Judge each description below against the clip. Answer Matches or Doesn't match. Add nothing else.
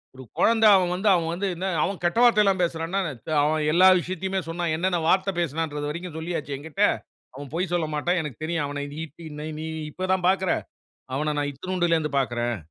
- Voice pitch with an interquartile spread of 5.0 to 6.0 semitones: Doesn't match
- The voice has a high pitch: Doesn't match